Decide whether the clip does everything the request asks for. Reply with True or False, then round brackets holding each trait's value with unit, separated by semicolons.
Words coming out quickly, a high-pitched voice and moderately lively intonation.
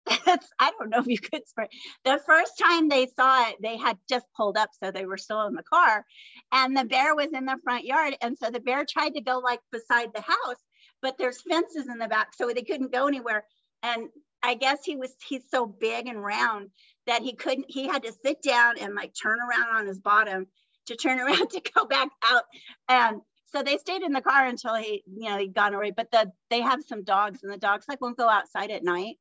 True (240 wpm; 245 Hz; 4.1 semitones)